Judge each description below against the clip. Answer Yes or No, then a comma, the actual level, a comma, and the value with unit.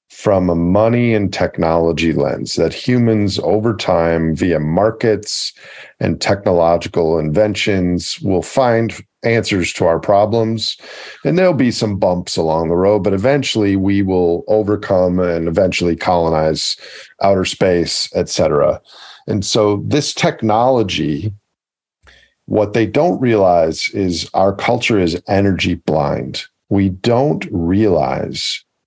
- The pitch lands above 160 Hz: No, low, 100 Hz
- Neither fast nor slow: No, slow, 120 wpm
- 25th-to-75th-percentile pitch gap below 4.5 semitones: Yes, average, 4.1 semitones